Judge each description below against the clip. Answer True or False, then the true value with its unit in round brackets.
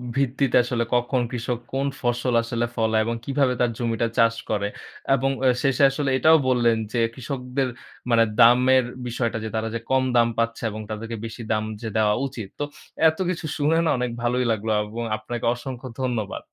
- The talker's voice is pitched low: True (120 Hz)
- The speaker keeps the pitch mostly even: True (2.3 semitones)